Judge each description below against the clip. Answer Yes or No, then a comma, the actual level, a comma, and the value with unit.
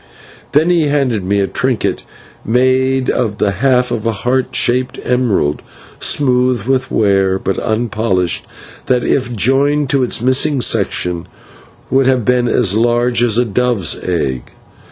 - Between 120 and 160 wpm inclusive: Yes, average, 145 wpm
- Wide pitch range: No, average, 3.9 semitones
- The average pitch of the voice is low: Yes, low, 125 Hz